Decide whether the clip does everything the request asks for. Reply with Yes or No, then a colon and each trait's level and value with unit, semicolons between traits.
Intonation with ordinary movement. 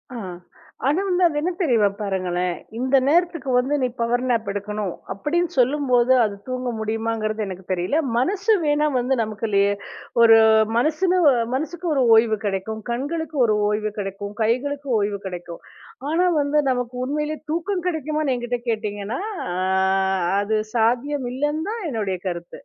No: wide, 6.0 semitones